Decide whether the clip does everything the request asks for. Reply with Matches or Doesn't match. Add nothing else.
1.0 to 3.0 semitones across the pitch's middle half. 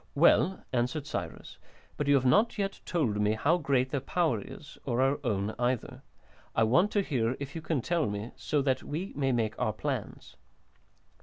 Doesn't match